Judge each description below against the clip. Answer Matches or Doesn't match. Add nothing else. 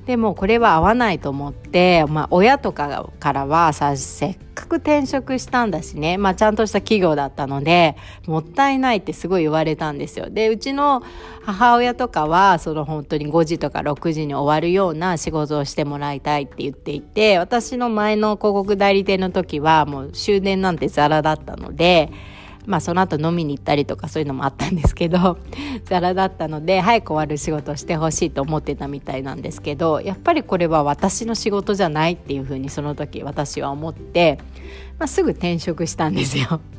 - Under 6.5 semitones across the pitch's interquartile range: Matches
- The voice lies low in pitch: Doesn't match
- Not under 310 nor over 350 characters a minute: Doesn't match